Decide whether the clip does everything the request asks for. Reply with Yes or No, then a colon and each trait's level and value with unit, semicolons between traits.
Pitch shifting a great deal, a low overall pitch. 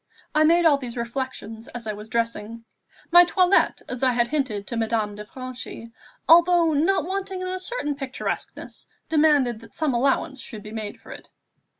No: wide, 6.0 semitones; very high, 260 Hz